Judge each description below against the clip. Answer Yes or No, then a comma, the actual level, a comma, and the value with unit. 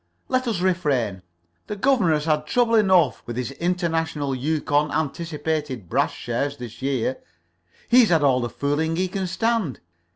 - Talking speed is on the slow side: No, average, 155 wpm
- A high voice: No, medium, 155 Hz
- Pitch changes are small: No, average, 5.1 semitones